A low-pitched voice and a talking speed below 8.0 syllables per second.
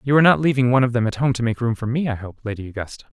No: low, 120 Hz; 8.1 syllables/s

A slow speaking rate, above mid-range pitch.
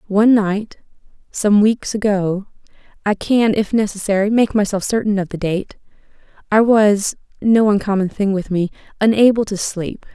Yes: slow, 125 wpm; high, 205 Hz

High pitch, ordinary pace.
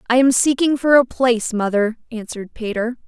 Yes: high, 240 Hz; average, 175 wpm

